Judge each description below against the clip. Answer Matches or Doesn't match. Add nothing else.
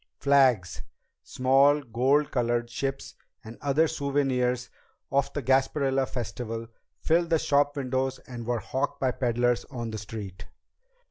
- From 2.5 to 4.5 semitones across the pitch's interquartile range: Matches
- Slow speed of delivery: Matches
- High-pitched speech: Doesn't match